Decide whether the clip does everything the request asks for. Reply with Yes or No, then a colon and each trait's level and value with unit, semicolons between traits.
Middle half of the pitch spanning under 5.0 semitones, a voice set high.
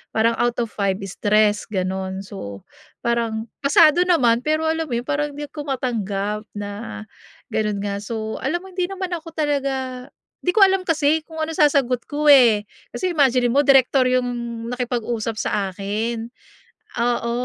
No: wide, 5.4 semitones; high, 245 Hz